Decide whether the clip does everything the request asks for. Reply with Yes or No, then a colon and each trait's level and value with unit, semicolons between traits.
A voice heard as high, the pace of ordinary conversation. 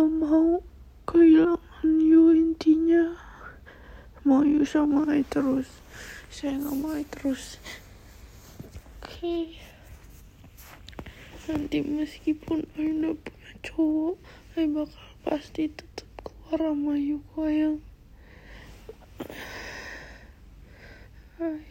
No: very high, 315 Hz; slow, 75 wpm